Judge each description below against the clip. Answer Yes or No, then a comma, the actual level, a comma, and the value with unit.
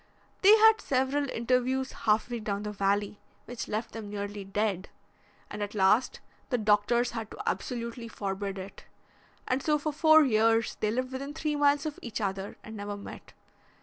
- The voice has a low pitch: No, high, 225 Hz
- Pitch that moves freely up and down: No, average, 4.3 semitones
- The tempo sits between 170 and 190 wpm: Yes, average, 175 wpm